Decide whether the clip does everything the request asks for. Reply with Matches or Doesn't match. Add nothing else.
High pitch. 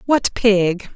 Matches